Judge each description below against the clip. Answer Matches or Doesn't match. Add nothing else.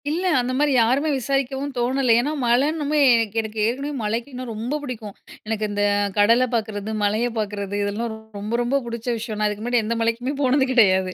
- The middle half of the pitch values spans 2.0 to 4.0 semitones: Matches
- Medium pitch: Doesn't match